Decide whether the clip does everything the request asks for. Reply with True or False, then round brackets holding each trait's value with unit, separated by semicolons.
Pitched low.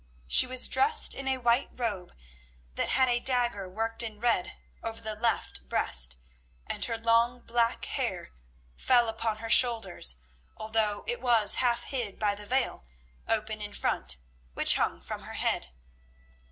False (230 Hz)